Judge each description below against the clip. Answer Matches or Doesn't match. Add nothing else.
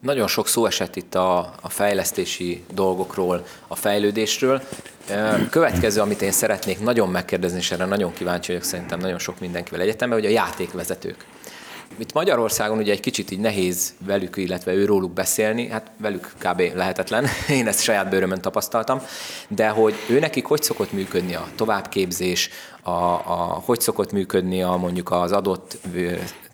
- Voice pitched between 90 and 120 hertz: Matches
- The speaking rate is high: Matches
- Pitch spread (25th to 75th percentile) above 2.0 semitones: Matches